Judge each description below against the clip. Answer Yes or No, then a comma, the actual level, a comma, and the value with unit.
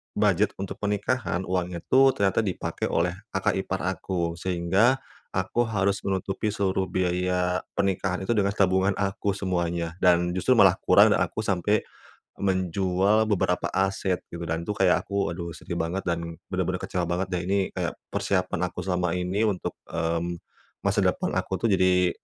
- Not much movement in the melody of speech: Yes, narrow, 2.0 semitones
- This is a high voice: No, very low, 95 Hz